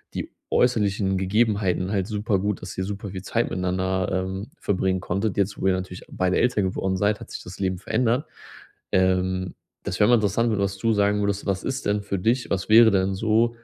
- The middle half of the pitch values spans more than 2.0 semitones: Yes, narrow, 2.4 semitones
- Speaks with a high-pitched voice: No, low, 100 Hz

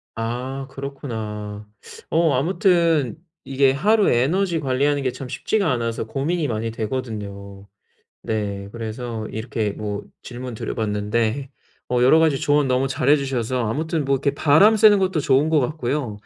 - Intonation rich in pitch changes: No, average, 4.8 semitones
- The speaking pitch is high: No, low, 130 Hz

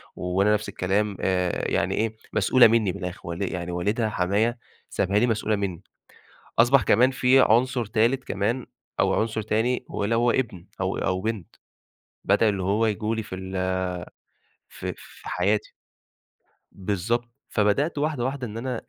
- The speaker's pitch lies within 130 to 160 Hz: No, low, 110 Hz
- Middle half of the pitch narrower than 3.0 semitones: No, average, 3.5 semitones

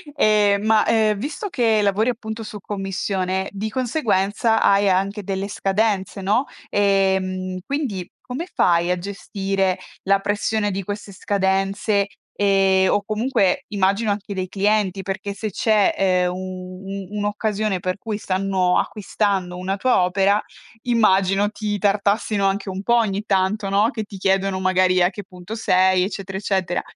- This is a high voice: Yes, high, 195 Hz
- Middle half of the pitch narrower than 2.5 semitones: Yes, narrow, 1.9 semitones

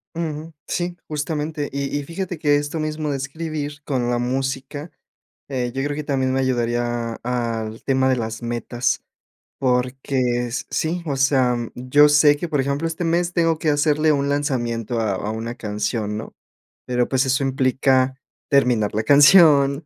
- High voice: No, low, 135 Hz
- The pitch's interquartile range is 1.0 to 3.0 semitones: No, average, 3.4 semitones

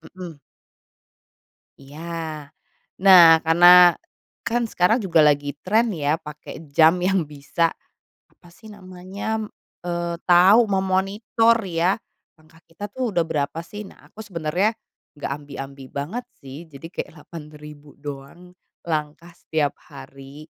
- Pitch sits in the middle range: Yes, medium, 170 Hz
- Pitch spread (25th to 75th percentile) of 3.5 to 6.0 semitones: Yes, average, 4.0 semitones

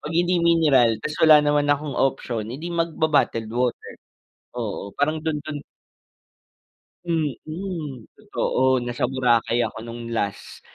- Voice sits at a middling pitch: Yes, medium, 145 Hz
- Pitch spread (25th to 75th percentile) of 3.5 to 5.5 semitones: Yes, average, 4.8 semitones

